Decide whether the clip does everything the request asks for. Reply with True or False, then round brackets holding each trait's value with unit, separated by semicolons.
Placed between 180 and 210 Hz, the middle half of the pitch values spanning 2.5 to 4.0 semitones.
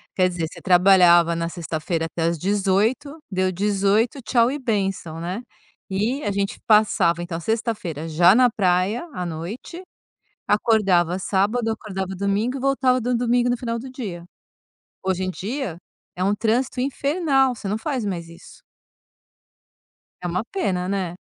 False (200 Hz; 5.1 semitones)